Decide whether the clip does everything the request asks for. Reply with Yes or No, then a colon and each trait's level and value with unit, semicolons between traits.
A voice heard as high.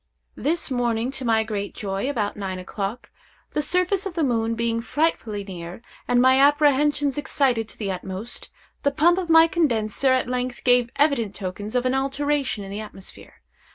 Yes: high, 245 Hz